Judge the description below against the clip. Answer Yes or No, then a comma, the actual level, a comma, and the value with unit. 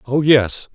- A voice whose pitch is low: Yes, low, 130 Hz